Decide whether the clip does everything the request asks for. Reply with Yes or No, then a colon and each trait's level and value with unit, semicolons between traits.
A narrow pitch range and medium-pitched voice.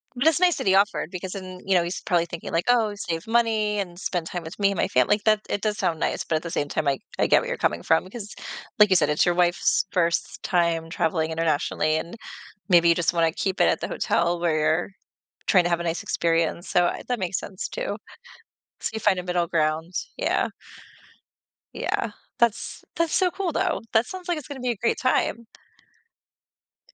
No: average, 4.2 semitones; medium, 180 Hz